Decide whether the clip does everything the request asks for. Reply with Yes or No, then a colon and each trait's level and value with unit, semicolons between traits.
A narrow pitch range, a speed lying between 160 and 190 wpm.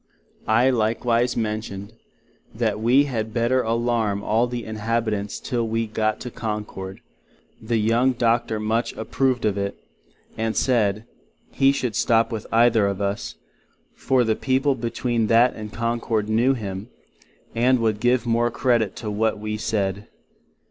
No: narrow, 2.0 semitones; average, 150 wpm